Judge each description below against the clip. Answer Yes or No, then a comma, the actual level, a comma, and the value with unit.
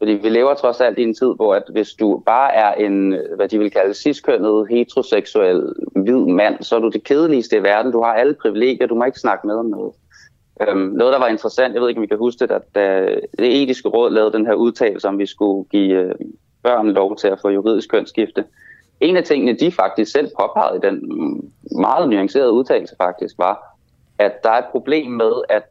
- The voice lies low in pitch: Yes, low, 120 Hz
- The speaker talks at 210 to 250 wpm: Yes, average, 215 wpm